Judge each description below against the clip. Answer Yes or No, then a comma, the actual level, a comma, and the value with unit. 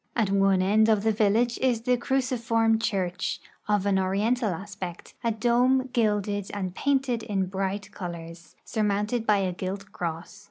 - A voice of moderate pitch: No, high, 205 Hz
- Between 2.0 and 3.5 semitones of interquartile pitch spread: Yes, average, 3.2 semitones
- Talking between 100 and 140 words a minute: No, average, 160 wpm